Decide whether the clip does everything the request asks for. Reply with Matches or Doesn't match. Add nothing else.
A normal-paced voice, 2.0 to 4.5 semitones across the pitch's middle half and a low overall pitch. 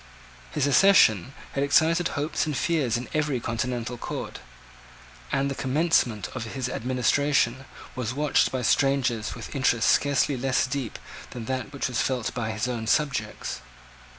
Matches